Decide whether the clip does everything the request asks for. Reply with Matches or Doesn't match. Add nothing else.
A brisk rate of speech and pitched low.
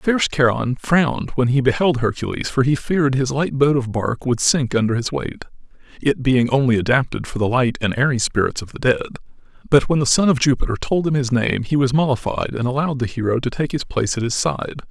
Matches